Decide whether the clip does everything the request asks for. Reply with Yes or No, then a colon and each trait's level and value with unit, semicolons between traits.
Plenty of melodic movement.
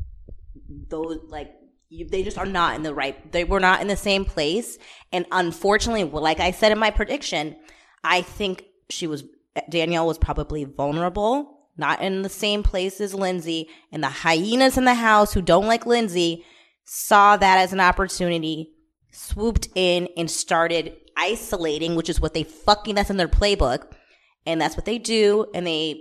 No: average, 4.4 semitones